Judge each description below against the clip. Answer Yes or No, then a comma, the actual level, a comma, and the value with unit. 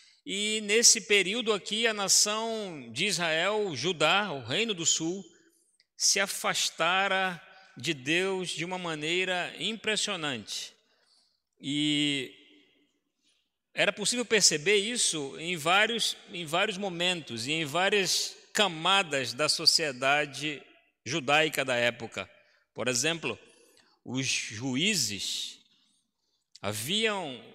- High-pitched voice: No, medium, 180 Hz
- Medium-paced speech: No, slow, 100 wpm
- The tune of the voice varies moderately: No, wide, 5.7 semitones